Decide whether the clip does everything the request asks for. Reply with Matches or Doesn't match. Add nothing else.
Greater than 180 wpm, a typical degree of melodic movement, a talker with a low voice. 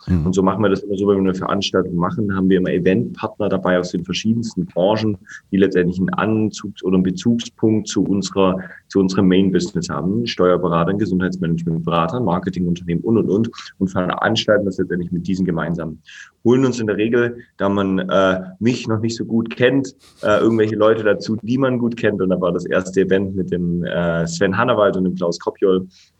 Matches